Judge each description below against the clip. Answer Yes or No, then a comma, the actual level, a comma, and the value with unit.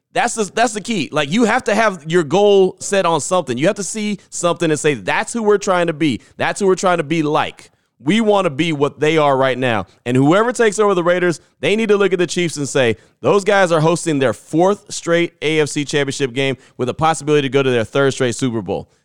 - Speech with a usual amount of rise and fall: No, wide, 5.7 semitones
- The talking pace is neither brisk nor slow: No, fast, 250 wpm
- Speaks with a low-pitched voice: No, medium, 165 Hz